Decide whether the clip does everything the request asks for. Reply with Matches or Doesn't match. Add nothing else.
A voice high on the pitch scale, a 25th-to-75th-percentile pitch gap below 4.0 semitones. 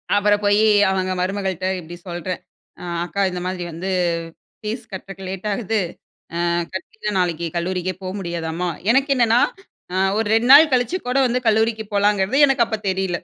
Matches